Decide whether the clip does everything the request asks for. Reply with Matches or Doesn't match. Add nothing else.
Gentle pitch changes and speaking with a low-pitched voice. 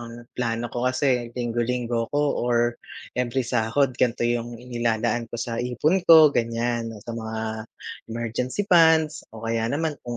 Matches